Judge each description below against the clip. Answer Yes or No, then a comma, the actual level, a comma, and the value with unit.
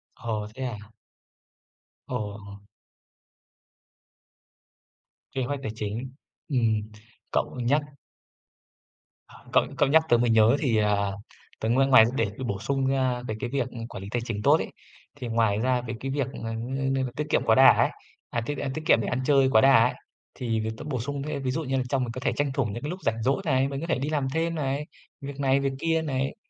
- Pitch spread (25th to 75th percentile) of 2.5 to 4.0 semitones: Yes, average, 3.5 semitones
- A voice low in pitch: Yes, low, 130 Hz